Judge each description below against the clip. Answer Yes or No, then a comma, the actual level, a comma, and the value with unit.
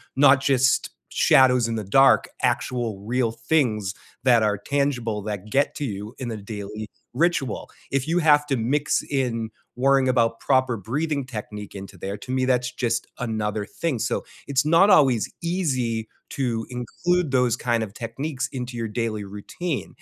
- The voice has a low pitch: Yes, low, 125 Hz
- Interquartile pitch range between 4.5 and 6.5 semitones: No, average, 3.8 semitones